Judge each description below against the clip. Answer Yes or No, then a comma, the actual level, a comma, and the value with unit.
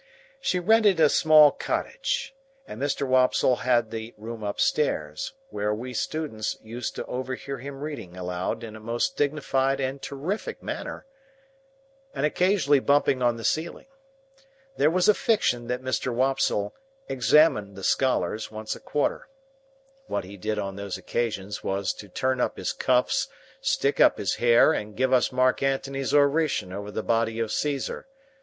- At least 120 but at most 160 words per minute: Yes, average, 155 wpm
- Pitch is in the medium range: No, low, 125 Hz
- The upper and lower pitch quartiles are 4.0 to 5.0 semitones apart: Yes, average, 4.7 semitones